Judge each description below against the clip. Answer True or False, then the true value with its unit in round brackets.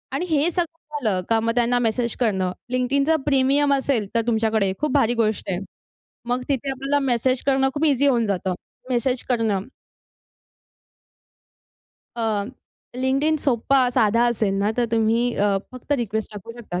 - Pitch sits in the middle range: False (240 Hz)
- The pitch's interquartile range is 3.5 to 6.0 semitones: True (3.8 semitones)